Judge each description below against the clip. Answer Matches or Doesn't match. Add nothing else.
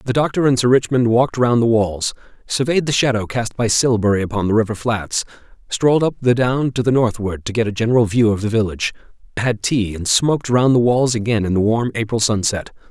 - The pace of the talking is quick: Matches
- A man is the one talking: Matches